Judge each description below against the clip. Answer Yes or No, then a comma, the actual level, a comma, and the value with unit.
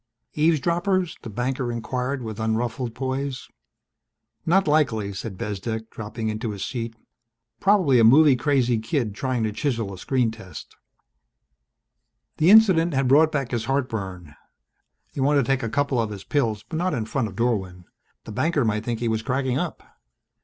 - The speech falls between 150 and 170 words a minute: Yes, average, 165 wpm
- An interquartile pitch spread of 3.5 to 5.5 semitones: Yes, average, 4.3 semitones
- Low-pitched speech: Yes, low, 120 Hz